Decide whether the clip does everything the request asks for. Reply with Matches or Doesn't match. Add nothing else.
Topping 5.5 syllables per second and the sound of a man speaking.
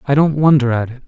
Matches